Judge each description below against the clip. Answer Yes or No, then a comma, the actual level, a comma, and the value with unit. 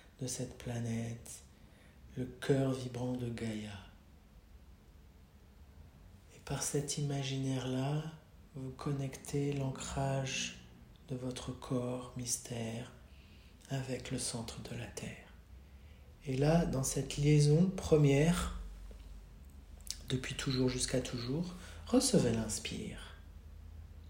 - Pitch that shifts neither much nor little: No, wide, 8.9 semitones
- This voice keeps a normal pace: No, slow, 90 wpm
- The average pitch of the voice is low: Yes, low, 125 Hz